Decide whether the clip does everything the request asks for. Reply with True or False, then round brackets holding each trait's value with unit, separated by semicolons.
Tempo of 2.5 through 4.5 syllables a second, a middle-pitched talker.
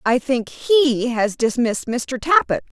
False (3.9 syllables/s; 255 Hz)